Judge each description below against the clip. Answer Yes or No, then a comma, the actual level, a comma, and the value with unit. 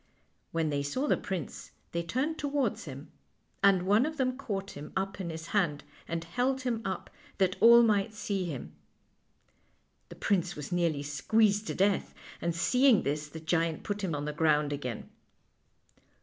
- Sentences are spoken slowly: No, average, 170 wpm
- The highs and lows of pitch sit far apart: Yes, wide, 5.8 semitones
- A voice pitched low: No, high, 190 Hz